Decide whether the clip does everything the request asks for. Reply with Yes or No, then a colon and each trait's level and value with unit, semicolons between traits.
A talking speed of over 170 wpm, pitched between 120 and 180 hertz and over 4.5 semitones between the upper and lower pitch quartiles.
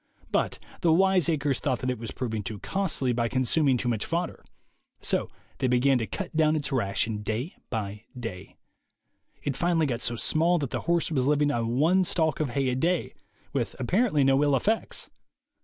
Yes: average, 190 wpm; low, 135 Hz; average, 5.2 semitones